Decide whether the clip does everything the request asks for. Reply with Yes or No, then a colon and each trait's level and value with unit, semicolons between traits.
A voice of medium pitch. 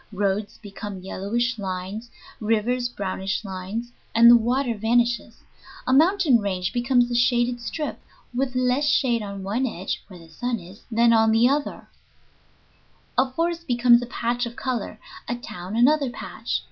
No: high, 235 Hz